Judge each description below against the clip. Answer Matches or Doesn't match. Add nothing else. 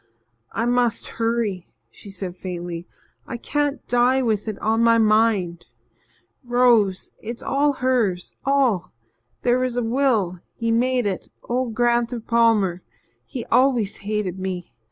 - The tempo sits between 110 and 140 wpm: Matches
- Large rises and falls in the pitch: Doesn't match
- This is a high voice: Matches